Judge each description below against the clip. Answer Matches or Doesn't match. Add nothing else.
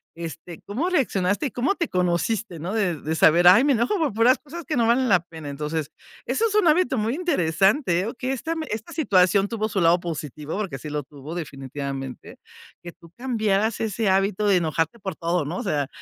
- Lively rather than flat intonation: Matches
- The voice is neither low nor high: Doesn't match